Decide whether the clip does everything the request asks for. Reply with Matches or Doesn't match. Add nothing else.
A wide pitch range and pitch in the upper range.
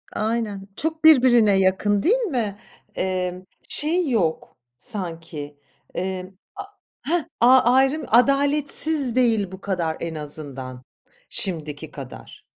Matches